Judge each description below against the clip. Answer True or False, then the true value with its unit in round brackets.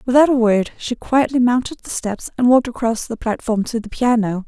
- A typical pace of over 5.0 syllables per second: True (5.5 syllables/s)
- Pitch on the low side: False (235 Hz)